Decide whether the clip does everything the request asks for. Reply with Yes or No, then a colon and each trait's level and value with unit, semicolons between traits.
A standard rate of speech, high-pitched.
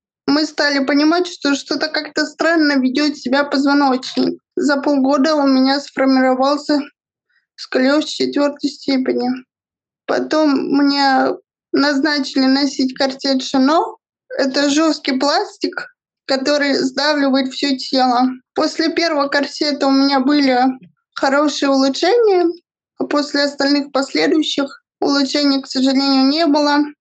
No: slow, 105 wpm; very high, 285 Hz